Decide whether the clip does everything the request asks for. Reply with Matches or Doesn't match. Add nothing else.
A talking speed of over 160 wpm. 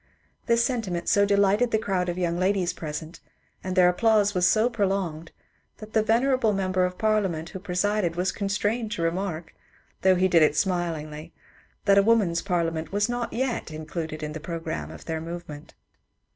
Matches